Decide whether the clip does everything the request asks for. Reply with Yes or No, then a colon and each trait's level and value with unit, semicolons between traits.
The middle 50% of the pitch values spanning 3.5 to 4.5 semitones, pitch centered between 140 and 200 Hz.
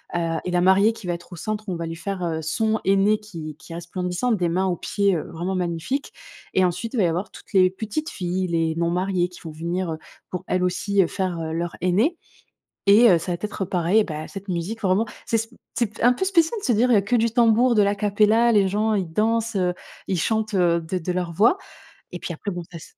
Yes: average, 3.9 semitones; high, 190 Hz